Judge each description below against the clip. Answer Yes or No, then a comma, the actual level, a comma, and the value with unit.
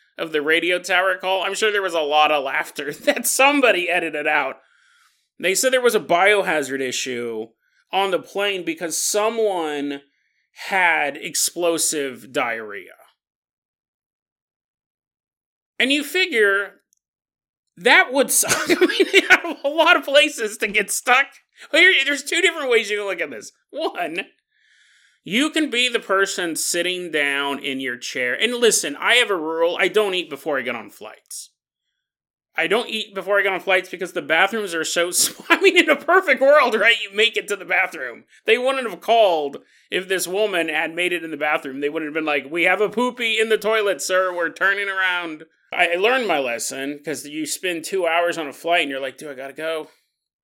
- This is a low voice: No, high, 190 Hz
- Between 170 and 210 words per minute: Yes, average, 190 wpm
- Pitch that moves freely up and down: Yes, wide, 7.0 semitones